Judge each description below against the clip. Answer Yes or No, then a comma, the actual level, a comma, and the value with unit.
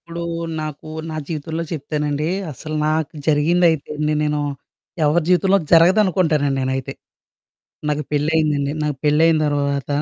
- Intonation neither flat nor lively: No, narrow, 2.0 semitones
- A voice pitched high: No, medium, 155 Hz